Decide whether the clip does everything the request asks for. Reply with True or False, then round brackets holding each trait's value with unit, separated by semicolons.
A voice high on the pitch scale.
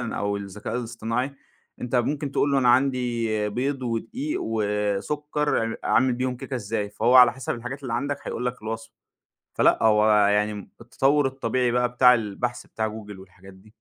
False (120 Hz)